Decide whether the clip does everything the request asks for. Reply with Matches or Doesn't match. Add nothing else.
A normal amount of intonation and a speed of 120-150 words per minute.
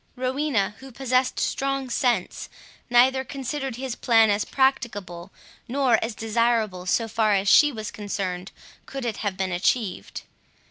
Matches